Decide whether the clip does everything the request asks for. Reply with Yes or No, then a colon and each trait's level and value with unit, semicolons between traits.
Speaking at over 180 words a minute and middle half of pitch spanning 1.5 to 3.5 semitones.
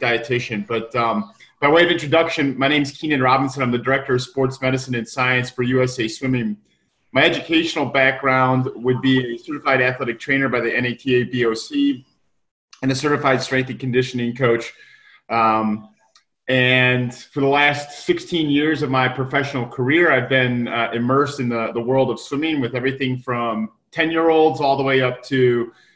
No: average, 175 wpm; average, 2.7 semitones